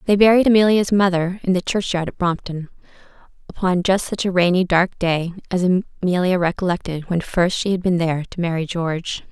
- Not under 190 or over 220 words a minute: No, average, 180 wpm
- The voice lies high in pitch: No, medium, 180 Hz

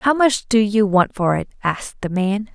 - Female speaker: Yes, female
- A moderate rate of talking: No, fast, 235 wpm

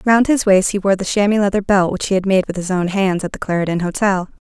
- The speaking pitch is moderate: No, high, 195 Hz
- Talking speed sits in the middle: No, fast, 280 wpm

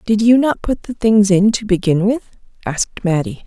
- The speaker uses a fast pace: Yes, fast, 210 wpm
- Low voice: No, high, 205 Hz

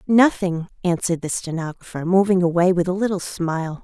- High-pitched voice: No, medium, 180 Hz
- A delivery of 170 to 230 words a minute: No, average, 155 wpm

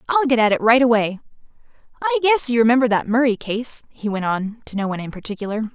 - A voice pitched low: No, high, 235 Hz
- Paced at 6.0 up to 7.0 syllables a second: Yes, 6.3 syllables/s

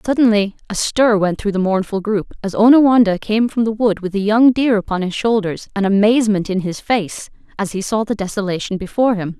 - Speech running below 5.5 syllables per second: No, 5.6 syllables/s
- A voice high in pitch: Yes, high, 210 Hz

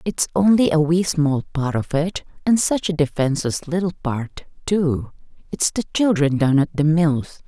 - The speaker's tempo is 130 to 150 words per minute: No, average, 170 wpm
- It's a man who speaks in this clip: No, female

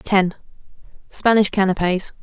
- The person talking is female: Yes, female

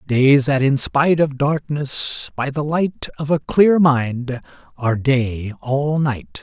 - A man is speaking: Yes, male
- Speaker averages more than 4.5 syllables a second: No, 3.5 syllables/s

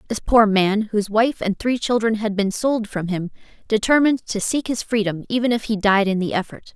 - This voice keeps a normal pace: No, fast, 220 wpm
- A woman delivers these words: Yes, female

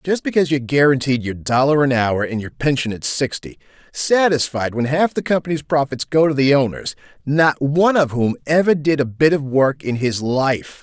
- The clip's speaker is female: No, male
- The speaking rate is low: No, average, 200 wpm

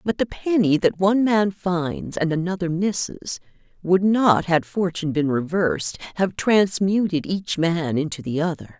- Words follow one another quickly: No, average, 155 wpm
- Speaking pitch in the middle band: Yes, medium, 175 Hz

